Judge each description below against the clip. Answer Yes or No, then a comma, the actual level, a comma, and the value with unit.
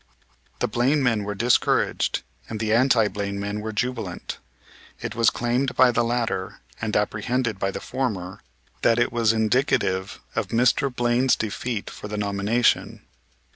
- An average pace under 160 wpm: Yes, average, 150 wpm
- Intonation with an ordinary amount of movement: Yes, average, 3.0 semitones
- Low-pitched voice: Yes, low, 115 Hz